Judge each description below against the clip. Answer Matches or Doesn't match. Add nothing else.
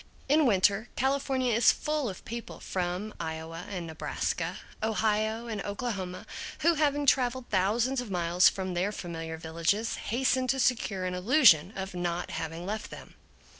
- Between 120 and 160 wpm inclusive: Matches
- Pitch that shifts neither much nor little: Doesn't match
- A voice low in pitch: Doesn't match